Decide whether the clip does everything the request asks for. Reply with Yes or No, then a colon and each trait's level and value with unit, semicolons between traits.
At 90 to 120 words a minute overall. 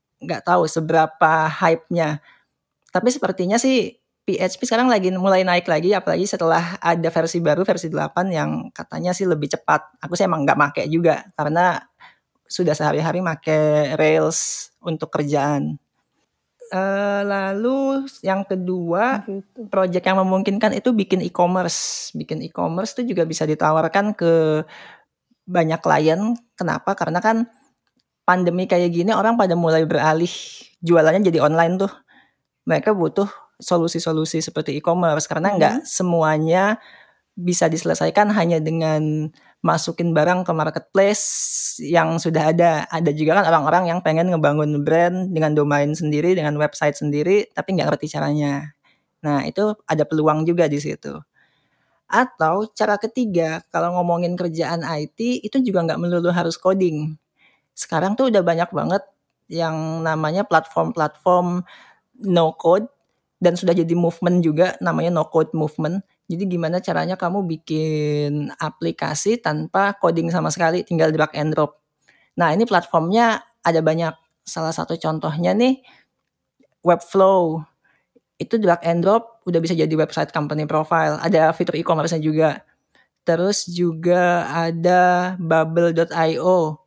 No: average, 130 wpm